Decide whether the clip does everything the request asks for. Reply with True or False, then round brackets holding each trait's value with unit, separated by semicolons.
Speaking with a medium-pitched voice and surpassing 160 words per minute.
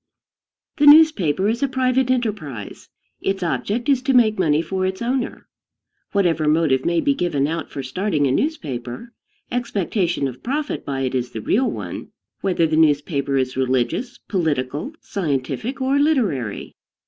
False (180 Hz; 150 wpm)